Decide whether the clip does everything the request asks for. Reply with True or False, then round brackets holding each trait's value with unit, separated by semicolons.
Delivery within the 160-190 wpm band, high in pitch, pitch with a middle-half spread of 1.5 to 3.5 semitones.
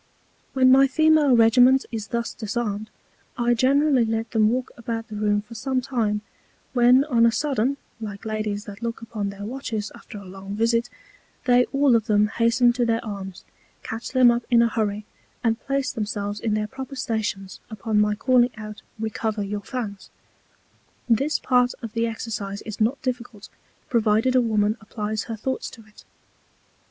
True (170 wpm; 230 Hz; 2.8 semitones)